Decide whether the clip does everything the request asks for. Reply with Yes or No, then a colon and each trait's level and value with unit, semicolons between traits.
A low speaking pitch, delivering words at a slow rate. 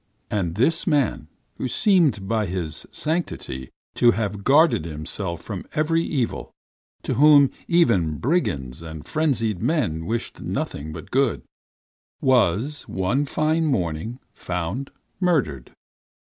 Yes: low, 115 Hz; slow, 115 wpm